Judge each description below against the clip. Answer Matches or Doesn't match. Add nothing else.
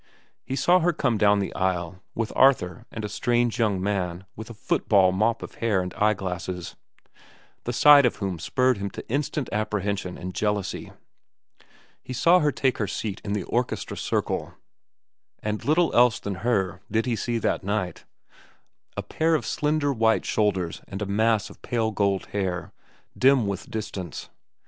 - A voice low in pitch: Matches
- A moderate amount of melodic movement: Matches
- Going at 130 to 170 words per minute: Matches